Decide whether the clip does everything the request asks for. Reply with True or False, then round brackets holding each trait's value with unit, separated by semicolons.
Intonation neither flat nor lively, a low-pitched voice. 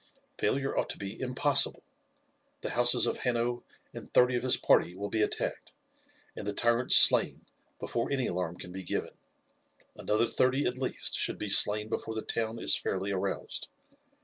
True (3.7 semitones; 115 Hz)